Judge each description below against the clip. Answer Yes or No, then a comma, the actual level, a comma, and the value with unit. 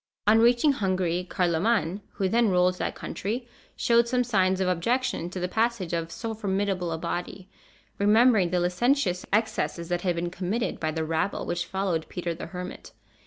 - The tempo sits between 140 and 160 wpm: No, average, 170 wpm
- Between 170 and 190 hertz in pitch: Yes, medium, 185 Hz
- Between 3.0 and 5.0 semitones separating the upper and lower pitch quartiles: Yes, average, 4.1 semitones